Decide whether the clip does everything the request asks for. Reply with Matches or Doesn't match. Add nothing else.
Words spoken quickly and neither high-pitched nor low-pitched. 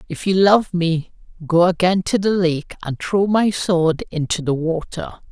Doesn't match